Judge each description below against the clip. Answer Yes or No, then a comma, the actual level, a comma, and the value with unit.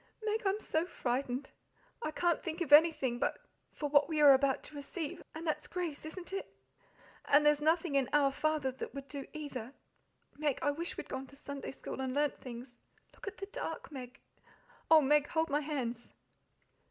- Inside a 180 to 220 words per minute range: Yes, average, 190 wpm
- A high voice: Yes, very high, 290 Hz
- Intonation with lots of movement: No, average, 2.8 semitones